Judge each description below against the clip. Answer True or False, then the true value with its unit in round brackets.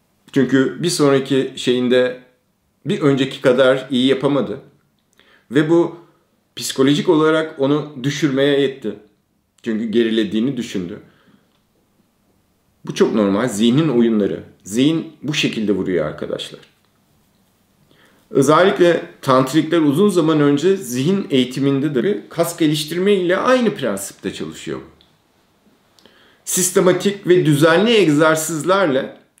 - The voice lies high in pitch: False (140 Hz)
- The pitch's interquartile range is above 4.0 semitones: True (5.0 semitones)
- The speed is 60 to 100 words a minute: True (95 wpm)